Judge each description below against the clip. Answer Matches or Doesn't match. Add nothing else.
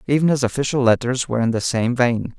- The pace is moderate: Doesn't match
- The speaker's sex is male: Matches